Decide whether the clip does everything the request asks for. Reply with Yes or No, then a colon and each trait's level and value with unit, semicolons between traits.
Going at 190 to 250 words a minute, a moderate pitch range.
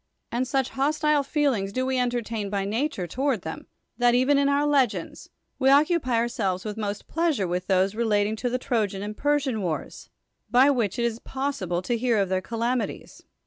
Yes: average, 195 wpm; average, 4.9 semitones